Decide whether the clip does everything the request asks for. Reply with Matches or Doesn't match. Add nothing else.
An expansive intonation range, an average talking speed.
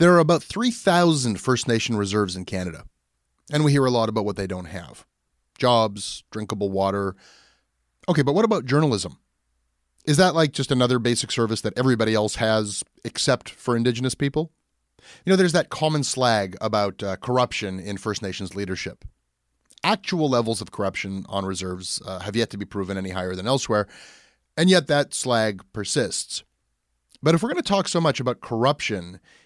Matches